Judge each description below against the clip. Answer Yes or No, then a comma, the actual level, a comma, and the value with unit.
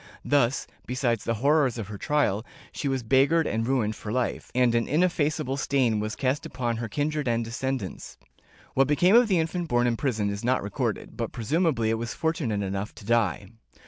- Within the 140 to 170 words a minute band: No, average, 190 wpm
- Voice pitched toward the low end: Yes, low, 125 Hz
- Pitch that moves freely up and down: No, average, 4.5 semitones